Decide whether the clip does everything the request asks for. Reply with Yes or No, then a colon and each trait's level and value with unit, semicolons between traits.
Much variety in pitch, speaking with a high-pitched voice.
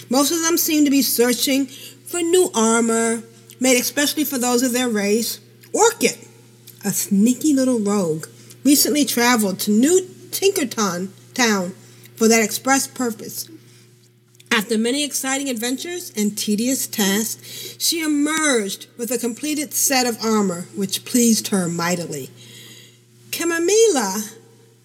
Yes: wide, 6.1 semitones; high, 230 Hz